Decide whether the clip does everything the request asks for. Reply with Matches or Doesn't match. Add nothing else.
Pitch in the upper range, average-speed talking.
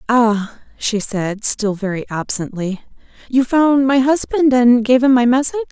Matches